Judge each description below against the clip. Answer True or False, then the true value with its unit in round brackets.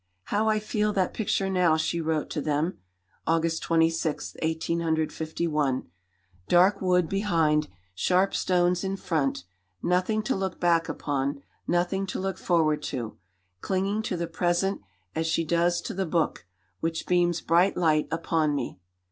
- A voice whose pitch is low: False (170 Hz)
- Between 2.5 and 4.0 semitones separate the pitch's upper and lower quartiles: True (2.9 semitones)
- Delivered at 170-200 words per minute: False (145 wpm)